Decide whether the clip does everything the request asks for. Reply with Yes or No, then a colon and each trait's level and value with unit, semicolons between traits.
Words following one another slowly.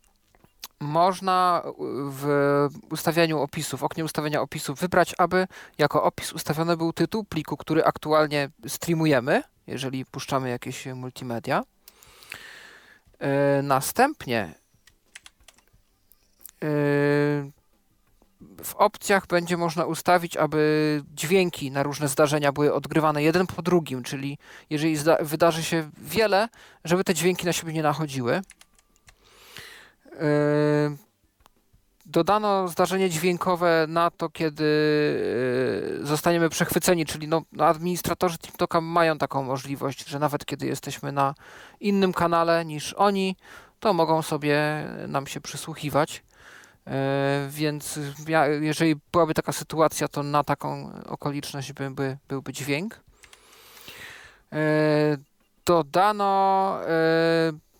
Yes: slow, 100 wpm